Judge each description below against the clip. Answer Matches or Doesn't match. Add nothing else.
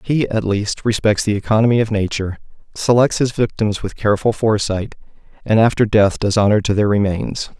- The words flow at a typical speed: Matches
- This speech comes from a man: Matches